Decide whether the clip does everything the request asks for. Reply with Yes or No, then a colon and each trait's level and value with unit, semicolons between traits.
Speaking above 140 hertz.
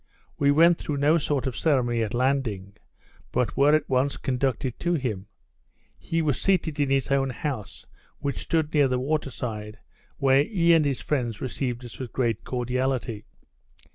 No: low, 135 Hz